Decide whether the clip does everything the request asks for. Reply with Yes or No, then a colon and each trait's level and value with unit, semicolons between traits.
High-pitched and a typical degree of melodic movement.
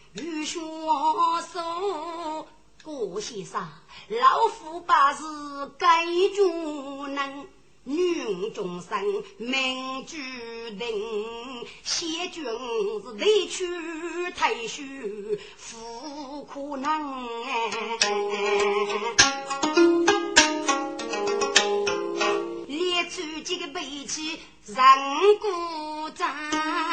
Yes: very high, 315 Hz; average, 4.6 semitones